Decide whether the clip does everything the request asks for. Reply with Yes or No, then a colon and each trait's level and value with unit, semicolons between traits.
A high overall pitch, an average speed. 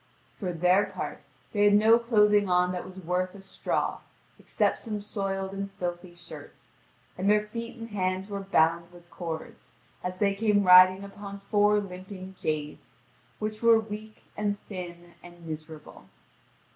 Yes: high, 195 Hz; average, 155 wpm